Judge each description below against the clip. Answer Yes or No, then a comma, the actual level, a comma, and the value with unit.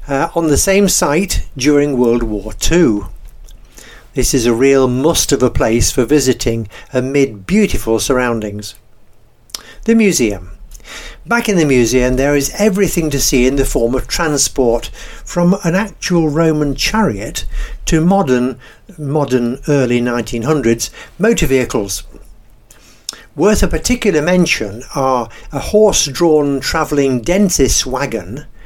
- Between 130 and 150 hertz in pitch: Yes, medium, 140 Hz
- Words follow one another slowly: Yes, slow, 130 wpm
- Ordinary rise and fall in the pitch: No, wide, 5.7 semitones